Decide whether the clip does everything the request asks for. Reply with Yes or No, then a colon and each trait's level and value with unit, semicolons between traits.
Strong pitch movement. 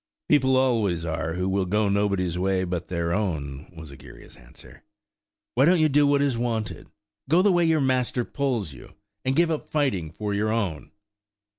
Yes: wide, 7.3 semitones